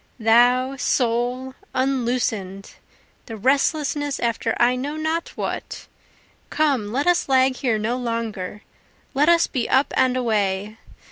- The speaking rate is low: Yes, slow, 125 wpm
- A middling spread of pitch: Yes, average, 3.3 semitones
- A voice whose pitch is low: No, very high, 250 Hz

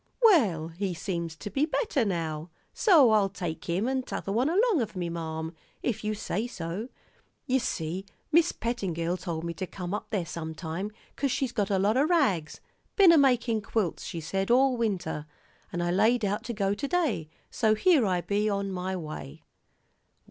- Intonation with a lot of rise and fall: Yes, wide, 6.3 semitones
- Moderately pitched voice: No, high, 200 Hz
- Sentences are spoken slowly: No, average, 185 wpm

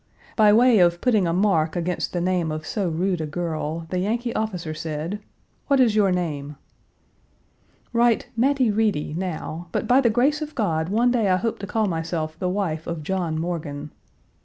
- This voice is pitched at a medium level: Yes, medium, 180 Hz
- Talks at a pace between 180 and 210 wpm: Yes, average, 185 wpm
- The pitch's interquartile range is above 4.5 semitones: Yes, average, 5.2 semitones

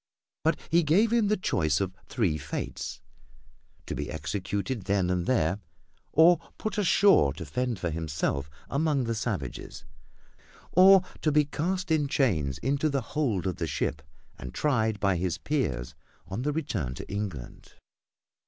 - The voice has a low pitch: Yes, low, 110 Hz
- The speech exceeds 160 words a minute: No, average, 155 wpm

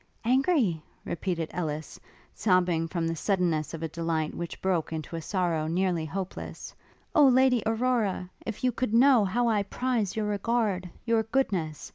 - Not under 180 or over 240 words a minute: No, average, 155 wpm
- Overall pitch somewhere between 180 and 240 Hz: Yes, high, 190 Hz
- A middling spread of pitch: No, wide, 5.8 semitones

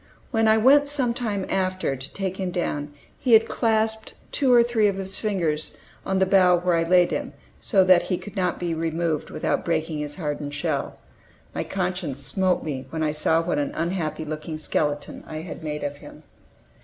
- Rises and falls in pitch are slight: No, average, 4.3 semitones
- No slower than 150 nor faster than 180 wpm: No, average, 195 wpm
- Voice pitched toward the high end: No, medium, 180 Hz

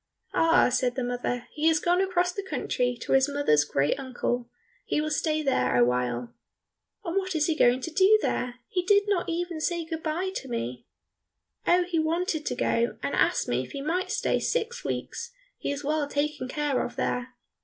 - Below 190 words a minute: No, average, 195 wpm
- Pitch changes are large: Yes, wide, 6.0 semitones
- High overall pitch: Yes, very high, 300 Hz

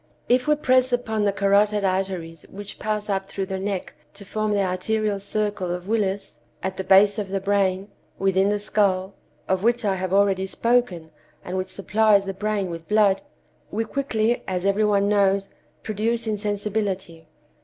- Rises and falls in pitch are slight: Yes, narrow, 2.0 semitones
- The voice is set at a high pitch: Yes, high, 200 Hz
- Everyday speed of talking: Yes, average, 165 wpm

